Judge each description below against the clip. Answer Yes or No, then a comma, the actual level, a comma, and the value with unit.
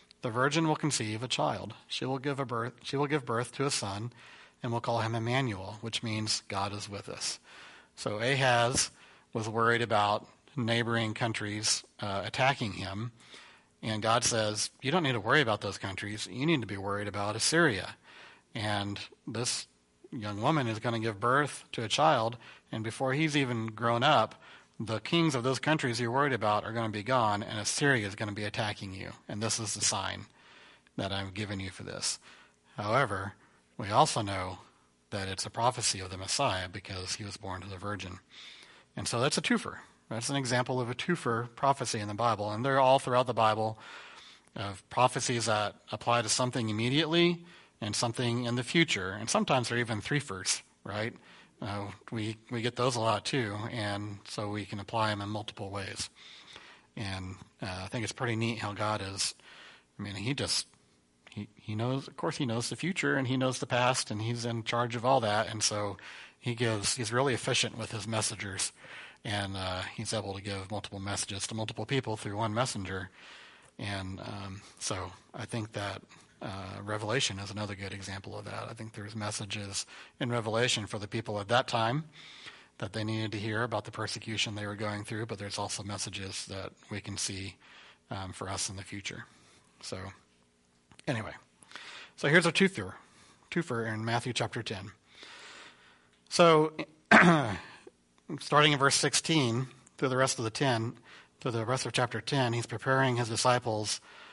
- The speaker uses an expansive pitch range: No, average, 3.5 semitones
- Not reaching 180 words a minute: No, average, 185 wpm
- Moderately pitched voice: No, low, 110 Hz